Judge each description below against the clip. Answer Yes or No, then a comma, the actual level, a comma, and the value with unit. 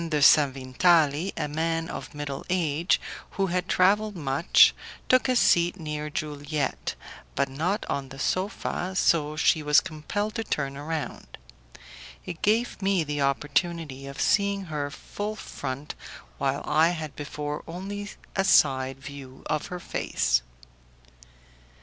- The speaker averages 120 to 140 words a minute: Yes, slow, 135 wpm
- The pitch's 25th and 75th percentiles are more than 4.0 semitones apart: Yes, average, 4.4 semitones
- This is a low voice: No, medium, 155 Hz